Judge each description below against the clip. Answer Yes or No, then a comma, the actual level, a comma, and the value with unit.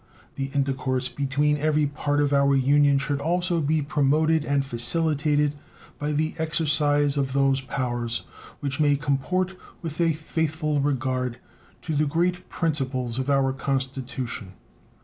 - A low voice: No, medium, 145 Hz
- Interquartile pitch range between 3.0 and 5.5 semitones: No, narrow, 2.4 semitones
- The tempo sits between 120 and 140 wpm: Yes, slow, 135 wpm